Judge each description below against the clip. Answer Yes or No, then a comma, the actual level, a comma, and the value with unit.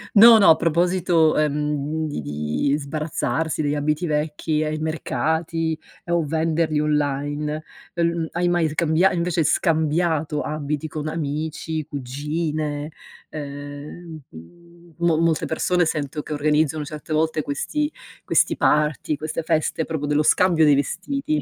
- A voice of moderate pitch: Yes, medium, 155 Hz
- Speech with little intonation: Yes, narrow, 1.9 semitones